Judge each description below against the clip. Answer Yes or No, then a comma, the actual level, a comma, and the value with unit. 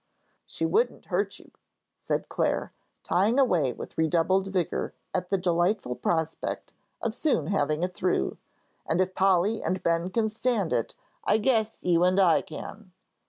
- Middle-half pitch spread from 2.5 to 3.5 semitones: No, average, 4.1 semitones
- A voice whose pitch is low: No, medium, 185 Hz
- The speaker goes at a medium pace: Yes, average, 155 wpm